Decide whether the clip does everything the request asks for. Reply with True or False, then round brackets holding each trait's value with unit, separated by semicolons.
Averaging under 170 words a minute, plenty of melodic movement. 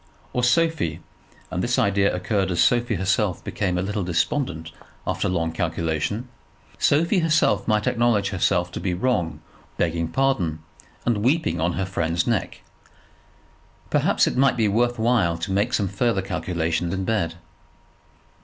True (145 wpm; 5.9 semitones)